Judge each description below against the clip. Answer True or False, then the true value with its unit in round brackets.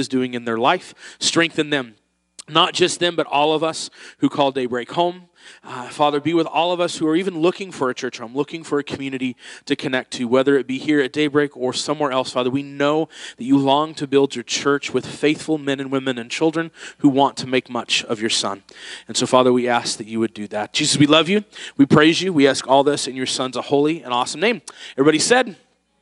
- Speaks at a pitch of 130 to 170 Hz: True (140 Hz)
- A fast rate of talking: True (240 wpm)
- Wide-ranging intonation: False (3.5 semitones)